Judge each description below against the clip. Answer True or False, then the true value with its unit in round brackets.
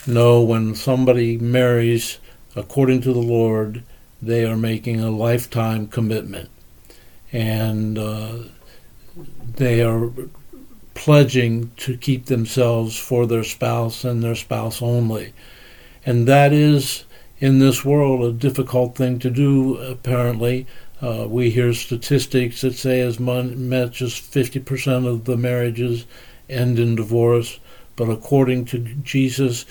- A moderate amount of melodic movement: False (1.8 semitones)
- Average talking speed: False (125 wpm)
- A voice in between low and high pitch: False (120 Hz)